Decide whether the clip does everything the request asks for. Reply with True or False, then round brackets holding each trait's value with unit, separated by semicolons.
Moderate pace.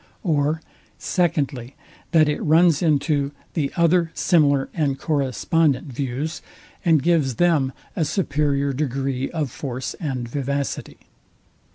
False (110 wpm)